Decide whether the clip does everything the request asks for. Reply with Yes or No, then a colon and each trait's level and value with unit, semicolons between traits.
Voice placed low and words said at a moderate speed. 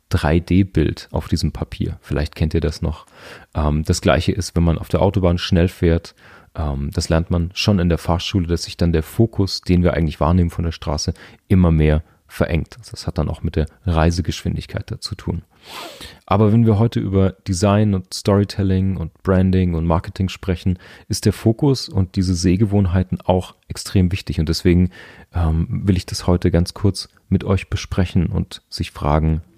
Yes: very low, 90 Hz; average, 175 wpm